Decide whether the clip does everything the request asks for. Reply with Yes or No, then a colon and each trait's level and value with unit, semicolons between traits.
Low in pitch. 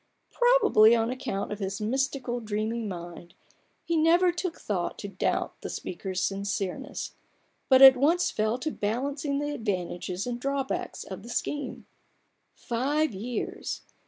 No: high, 240 Hz